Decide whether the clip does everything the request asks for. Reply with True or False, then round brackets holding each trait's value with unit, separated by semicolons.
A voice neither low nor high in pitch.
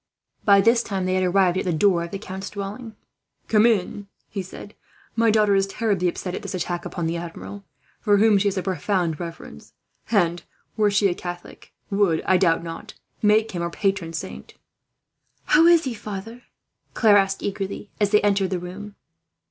False (195 Hz)